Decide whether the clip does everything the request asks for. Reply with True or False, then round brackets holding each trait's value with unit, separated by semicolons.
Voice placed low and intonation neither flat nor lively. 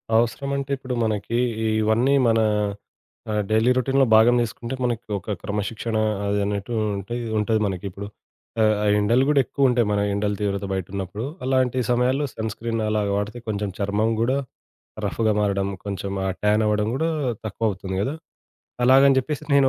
True (110 Hz; 3.2 semitones)